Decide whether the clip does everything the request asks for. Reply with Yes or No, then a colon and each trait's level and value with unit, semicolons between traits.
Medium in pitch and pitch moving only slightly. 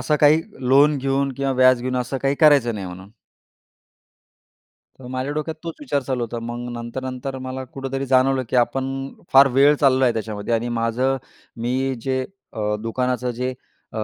No: low, 130 Hz; narrow, 2.0 semitones